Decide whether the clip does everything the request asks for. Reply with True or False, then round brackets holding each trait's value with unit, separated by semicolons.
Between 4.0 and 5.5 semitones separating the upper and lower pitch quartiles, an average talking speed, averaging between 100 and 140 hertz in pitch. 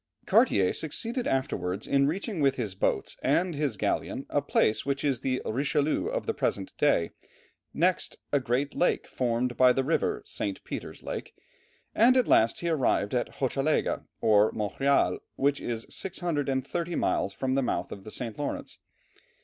True (4.7 semitones; 160 wpm; 135 Hz)